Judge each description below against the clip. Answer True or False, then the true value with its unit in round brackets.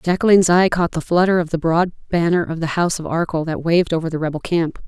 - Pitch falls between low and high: True (170 Hz)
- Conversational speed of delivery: False (245 wpm)